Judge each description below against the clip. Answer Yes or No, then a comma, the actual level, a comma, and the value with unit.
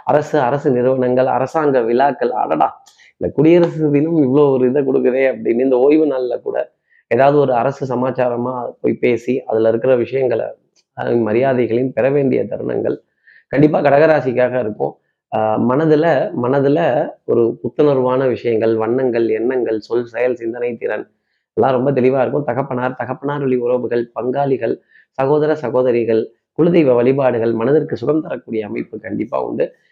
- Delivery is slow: No, fast, 130 wpm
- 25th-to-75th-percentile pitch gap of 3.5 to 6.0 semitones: No, average, 3.1 semitones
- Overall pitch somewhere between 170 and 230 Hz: No, low, 130 Hz